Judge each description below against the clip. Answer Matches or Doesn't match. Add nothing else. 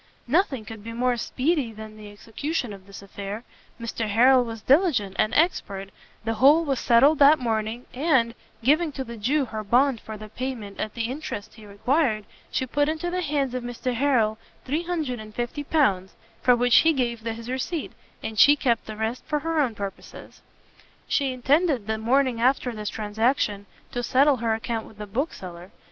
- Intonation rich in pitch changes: Doesn't match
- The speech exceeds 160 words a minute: Matches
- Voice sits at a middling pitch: Doesn't match